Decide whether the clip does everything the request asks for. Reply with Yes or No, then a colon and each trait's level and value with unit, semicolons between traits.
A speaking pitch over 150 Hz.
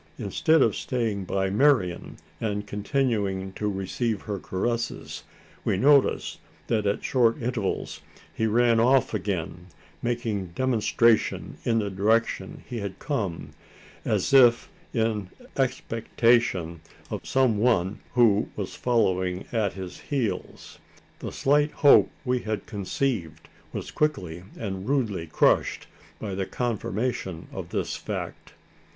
No: low, 110 Hz